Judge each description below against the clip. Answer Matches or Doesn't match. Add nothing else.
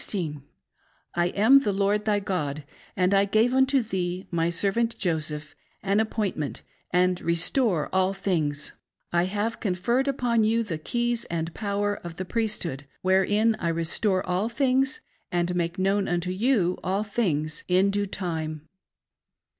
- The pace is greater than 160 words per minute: Doesn't match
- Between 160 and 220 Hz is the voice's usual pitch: Matches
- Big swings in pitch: Doesn't match